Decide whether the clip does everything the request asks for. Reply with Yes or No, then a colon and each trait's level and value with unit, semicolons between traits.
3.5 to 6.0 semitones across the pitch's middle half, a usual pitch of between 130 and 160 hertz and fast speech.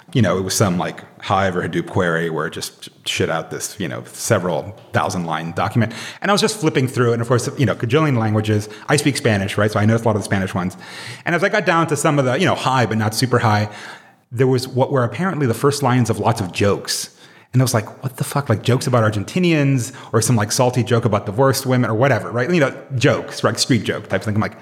No: average, 4.1 semitones; low, 120 Hz; fast, 270 wpm